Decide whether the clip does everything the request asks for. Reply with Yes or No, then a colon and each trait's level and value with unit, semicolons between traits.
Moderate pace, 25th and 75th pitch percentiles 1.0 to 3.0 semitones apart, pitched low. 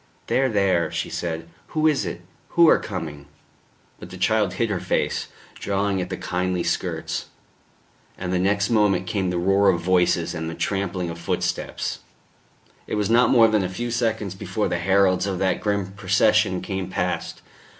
Yes: average, 175 wpm; narrow, 2.6 semitones; very low, 95 Hz